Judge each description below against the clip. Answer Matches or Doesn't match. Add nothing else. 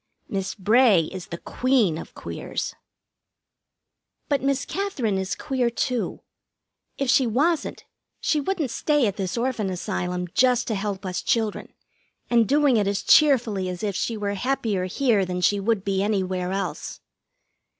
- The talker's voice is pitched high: Matches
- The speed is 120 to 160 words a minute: Matches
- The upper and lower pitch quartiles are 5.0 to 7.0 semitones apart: Matches